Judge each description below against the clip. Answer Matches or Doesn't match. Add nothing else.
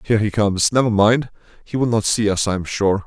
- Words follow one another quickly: Matches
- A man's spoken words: Matches